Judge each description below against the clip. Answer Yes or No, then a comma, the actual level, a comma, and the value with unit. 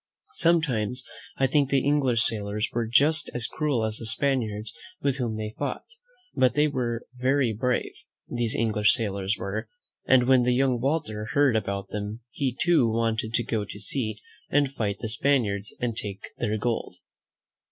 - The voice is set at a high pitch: No, low, 120 Hz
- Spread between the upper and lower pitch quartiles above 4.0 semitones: No, average, 3.7 semitones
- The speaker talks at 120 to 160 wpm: No, average, 175 wpm